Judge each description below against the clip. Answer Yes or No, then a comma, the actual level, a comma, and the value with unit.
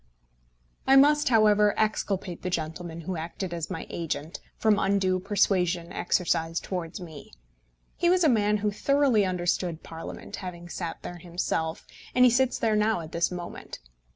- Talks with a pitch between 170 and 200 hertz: Yes, medium, 185 Hz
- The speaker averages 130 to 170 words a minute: Yes, average, 155 wpm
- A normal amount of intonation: Yes, average, 3.9 semitones